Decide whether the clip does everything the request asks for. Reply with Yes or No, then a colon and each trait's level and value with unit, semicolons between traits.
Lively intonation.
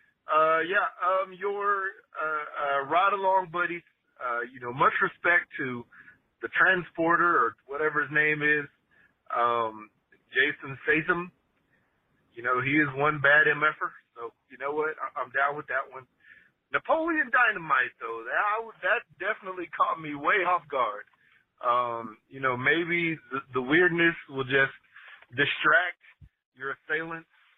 No: average, 4.8 semitones